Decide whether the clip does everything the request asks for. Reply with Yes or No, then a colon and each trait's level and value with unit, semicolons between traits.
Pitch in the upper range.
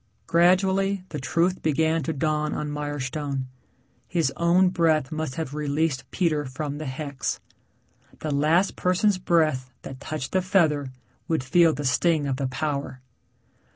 No: medium, 155 Hz